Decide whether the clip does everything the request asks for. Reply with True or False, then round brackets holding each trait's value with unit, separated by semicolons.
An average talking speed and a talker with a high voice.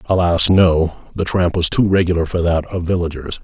False (190 wpm; 85 Hz)